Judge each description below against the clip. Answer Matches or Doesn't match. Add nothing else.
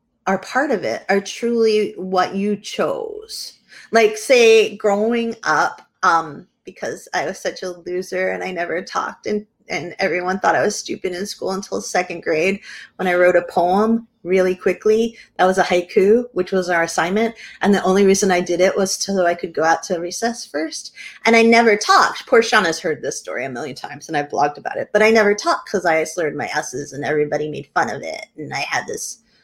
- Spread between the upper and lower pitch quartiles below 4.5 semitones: Matches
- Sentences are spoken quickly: Matches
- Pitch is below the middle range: Doesn't match